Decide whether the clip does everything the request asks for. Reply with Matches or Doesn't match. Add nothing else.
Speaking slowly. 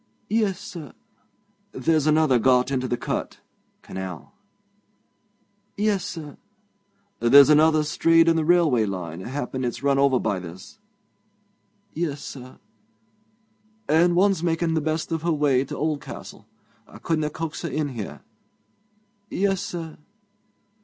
Matches